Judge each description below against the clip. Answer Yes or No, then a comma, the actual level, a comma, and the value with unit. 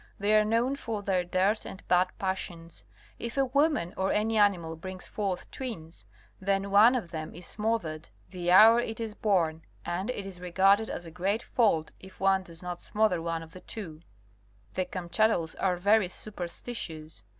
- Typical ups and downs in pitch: Yes, average, 3.8 semitones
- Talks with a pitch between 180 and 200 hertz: Yes, high, 190 Hz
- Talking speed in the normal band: Yes, average, 175 wpm